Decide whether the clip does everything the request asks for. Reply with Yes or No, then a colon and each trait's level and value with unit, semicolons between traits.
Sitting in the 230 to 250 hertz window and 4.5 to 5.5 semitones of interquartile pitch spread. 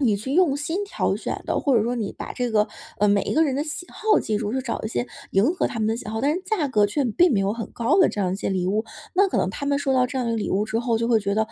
Yes: high, 235 Hz; average, 5.2 semitones